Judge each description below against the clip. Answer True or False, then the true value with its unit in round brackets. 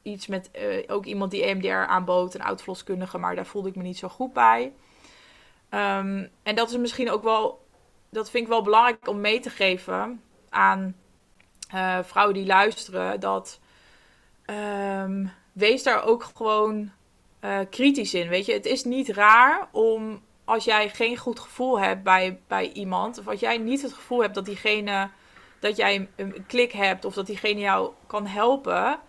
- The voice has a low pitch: False (205 Hz)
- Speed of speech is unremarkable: True (175 wpm)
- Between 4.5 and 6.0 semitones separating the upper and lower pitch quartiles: False (3.4 semitones)